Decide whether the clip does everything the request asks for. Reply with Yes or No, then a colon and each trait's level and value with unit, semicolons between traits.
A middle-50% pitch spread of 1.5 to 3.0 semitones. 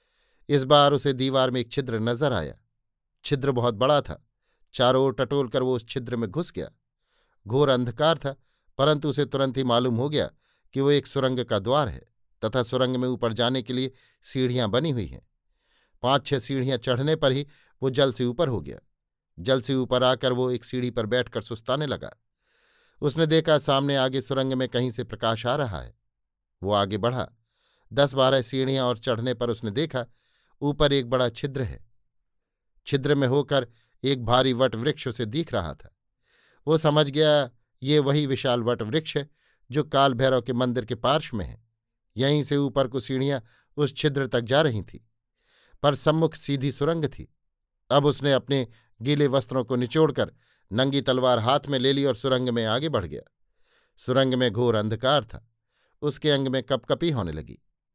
Yes: average, 2.7 semitones